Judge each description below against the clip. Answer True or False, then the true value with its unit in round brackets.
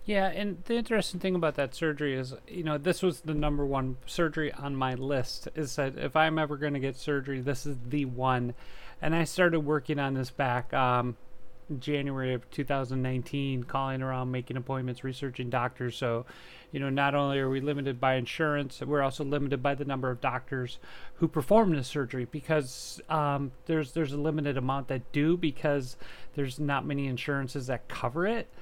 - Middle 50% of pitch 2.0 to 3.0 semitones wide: True (2.6 semitones)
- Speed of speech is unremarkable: True (185 wpm)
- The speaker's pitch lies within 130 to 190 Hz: True (140 Hz)